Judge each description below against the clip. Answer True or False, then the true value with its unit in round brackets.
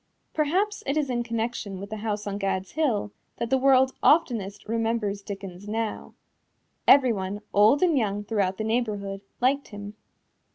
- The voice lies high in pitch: True (220 Hz)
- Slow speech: False (155 wpm)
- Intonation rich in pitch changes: False (4.2 semitones)